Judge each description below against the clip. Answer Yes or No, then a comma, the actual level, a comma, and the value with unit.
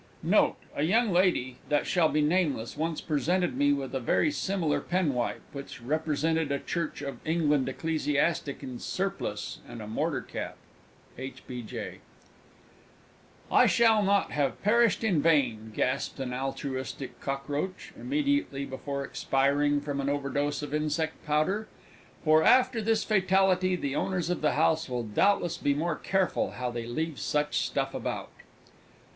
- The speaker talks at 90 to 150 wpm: Yes, average, 145 wpm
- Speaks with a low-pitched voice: No, medium, 150 Hz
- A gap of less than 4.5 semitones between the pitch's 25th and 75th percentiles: No, average, 4.8 semitones